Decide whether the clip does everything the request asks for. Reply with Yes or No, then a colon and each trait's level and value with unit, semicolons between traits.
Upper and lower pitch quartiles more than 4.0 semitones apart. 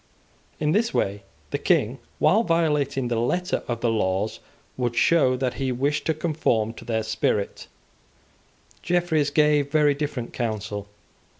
Yes: average, 5.2 semitones